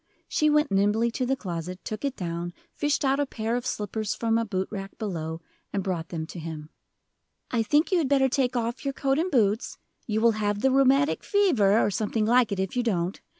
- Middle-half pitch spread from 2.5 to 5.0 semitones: No, wide, 5.5 semitones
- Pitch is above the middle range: Yes, high, 225 Hz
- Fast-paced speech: Yes, fast, 220 wpm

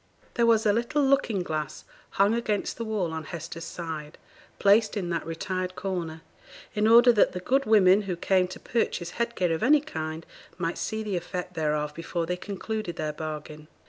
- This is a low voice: No, medium, 185 Hz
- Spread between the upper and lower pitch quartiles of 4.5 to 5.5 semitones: Yes, average, 4.9 semitones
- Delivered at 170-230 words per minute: Yes, average, 185 wpm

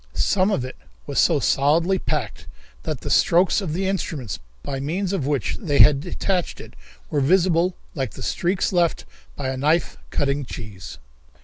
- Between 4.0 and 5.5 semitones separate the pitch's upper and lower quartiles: Yes, average, 5.2 semitones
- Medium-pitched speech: Yes, medium, 155 Hz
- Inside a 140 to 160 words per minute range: No, average, 170 wpm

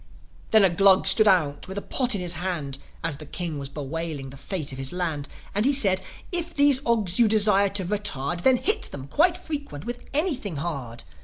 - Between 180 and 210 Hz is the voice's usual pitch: Yes, medium, 185 Hz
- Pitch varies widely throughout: Yes, wide, 7.5 semitones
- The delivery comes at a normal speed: No, fast, 210 wpm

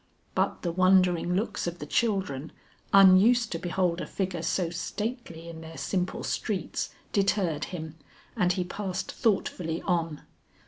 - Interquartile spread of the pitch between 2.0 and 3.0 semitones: Yes, average, 2.7 semitones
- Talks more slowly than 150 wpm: Yes, average, 140 wpm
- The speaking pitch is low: No, medium, 180 Hz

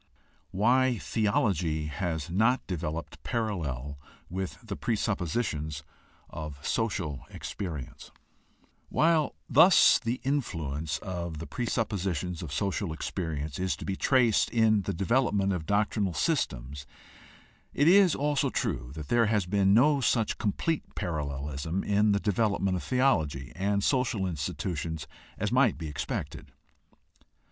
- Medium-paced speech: No, slow, 125 wpm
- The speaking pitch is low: Yes, very low, 95 Hz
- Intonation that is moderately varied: No, wide, 6.4 semitones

